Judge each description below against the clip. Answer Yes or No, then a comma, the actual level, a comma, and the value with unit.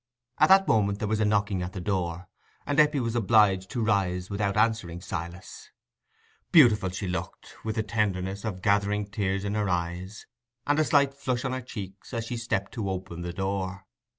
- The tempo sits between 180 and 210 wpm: Yes, average, 190 wpm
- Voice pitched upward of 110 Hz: No, low, 100 Hz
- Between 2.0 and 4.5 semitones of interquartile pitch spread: Yes, average, 3.3 semitones